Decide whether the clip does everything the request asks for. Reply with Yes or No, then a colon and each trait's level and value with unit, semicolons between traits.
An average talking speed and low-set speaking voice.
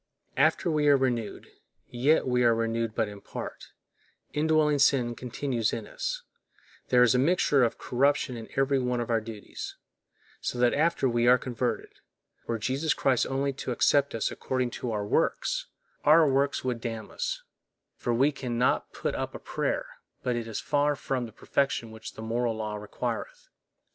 Yes: average, 175 wpm; low, 125 Hz